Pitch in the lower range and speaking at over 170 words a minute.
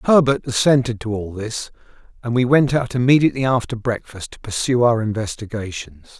No: low, 120 Hz; average, 155 wpm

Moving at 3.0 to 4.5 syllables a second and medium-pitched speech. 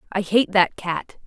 No: 4.1 syllables/s; high, 195 Hz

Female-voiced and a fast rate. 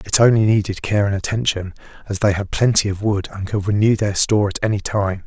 No: male; fast, 230 wpm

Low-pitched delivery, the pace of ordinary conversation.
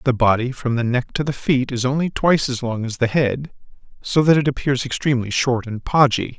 No: low, 130 Hz; fast, 225 wpm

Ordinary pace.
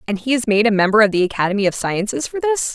No: fast, 285 wpm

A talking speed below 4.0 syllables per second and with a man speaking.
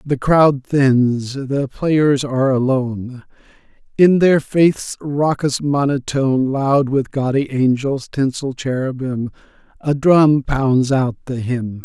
Yes: 3.5 syllables/s; male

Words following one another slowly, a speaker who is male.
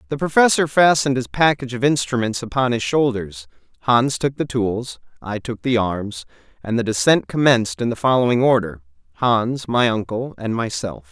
No: average, 165 wpm; male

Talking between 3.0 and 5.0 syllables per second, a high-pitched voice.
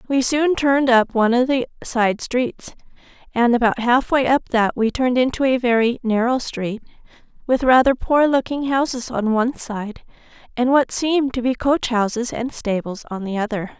Yes: 4.9 syllables/s; high, 245 Hz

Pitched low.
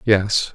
Yes: low, 100 Hz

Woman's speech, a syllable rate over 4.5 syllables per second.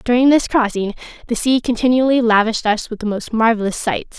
Yes: female; 5.9 syllables/s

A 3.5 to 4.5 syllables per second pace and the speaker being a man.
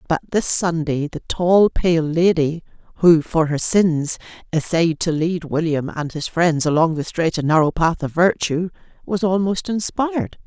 No: 4.3 syllables/s; female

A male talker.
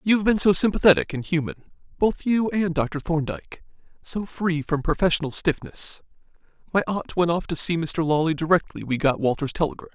Yes: male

